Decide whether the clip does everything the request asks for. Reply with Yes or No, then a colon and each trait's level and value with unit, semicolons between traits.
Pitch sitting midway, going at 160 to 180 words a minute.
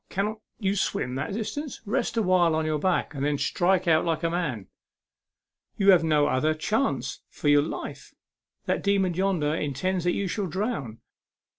Yes: medium, 175 Hz; average, 170 wpm